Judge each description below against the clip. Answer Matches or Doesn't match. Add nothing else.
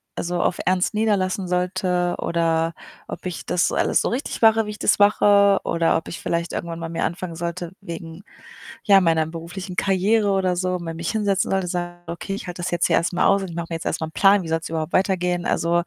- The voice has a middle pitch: Matches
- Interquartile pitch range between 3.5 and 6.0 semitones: Doesn't match